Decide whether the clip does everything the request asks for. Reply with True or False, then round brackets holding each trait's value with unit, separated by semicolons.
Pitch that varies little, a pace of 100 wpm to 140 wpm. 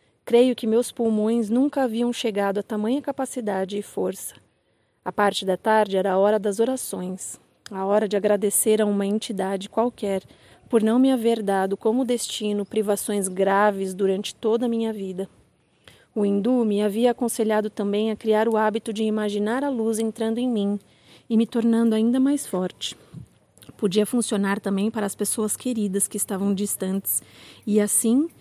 False (2.3 semitones; 165 wpm)